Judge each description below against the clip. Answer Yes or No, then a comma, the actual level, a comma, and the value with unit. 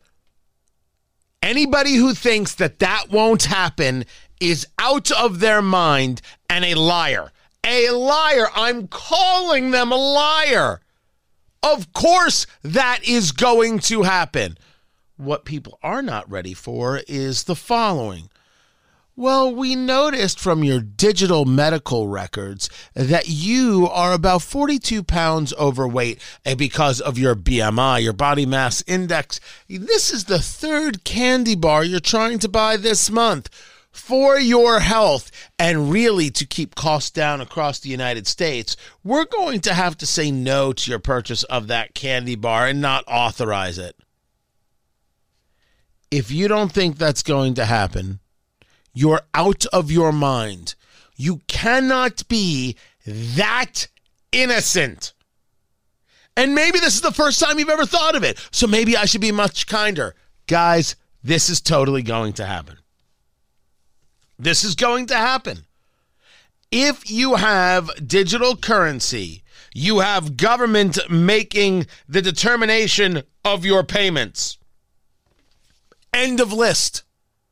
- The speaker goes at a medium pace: No, slow, 130 wpm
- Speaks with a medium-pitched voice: Yes, medium, 180 Hz